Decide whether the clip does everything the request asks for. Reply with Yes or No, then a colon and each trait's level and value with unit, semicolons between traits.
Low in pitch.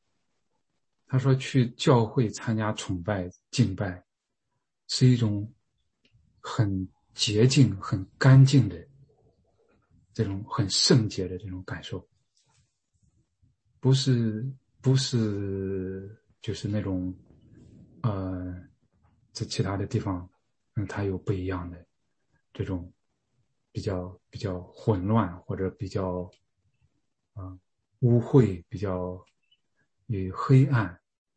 Yes: low, 105 Hz